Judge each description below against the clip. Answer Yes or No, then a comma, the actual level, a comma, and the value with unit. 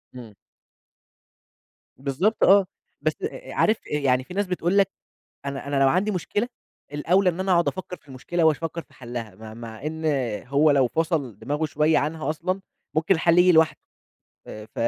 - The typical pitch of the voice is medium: Yes, medium, 160 Hz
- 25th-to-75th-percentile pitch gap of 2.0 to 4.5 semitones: No, average, 5.0 semitones